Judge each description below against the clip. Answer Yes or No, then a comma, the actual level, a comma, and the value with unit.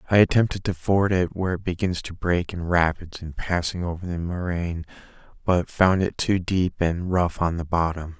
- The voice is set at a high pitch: No, very low, 90 Hz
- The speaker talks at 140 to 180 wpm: No, average, 200 wpm